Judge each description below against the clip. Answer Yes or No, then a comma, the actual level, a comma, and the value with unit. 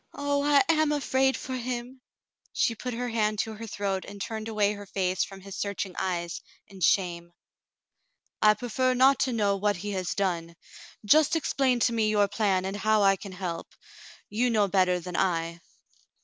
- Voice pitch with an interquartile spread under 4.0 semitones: No, average, 4.4 semitones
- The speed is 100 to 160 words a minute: No, average, 180 wpm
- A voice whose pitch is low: No, high, 205 Hz